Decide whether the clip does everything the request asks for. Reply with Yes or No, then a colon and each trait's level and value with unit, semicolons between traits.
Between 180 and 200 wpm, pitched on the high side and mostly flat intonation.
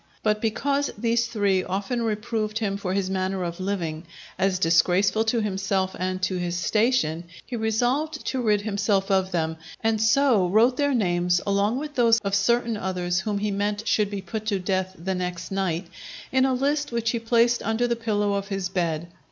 No: average, 190 wpm; high, 205 Hz; average, 3.5 semitones